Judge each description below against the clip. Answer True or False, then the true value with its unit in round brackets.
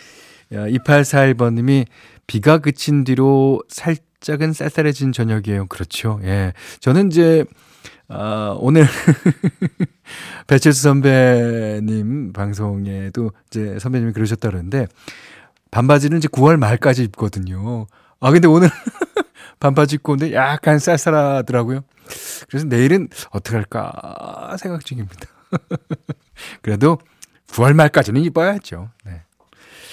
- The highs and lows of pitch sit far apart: True (5.9 semitones)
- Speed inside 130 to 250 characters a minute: True (240 characters per minute)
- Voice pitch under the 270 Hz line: True (135 Hz)